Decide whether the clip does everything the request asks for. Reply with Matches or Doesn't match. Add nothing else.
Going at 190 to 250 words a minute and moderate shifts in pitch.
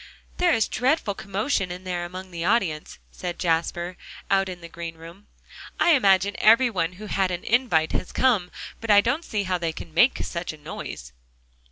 Matches